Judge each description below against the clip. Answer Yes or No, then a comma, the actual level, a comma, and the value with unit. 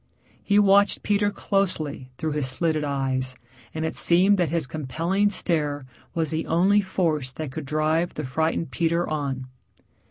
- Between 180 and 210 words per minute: No, average, 155 wpm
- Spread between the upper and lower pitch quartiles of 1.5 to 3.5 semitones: No, average, 3.9 semitones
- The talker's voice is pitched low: No, medium, 160 Hz